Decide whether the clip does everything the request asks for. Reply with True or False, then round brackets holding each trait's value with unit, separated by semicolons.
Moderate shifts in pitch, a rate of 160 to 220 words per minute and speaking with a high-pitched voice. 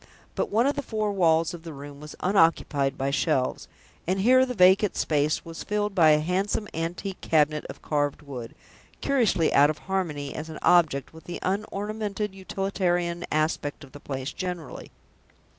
False (4.6 semitones; 170 wpm; 170 Hz)